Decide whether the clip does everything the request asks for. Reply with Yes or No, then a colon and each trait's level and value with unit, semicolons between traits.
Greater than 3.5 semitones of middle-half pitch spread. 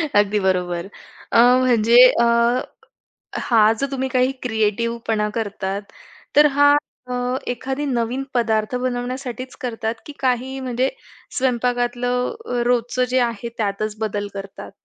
No: average, 2.9 semitones